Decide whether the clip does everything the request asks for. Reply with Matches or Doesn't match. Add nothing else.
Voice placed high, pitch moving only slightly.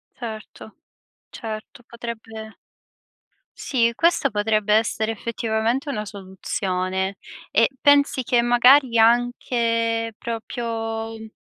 Matches